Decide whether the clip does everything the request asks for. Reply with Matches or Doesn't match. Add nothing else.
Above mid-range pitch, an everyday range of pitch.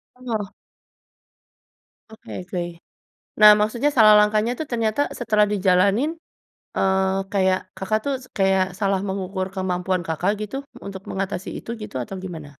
Doesn't match